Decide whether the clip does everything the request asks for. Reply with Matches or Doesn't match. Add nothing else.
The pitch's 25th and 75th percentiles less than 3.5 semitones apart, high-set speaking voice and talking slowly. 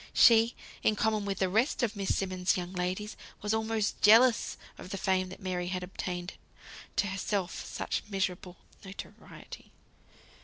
Doesn't match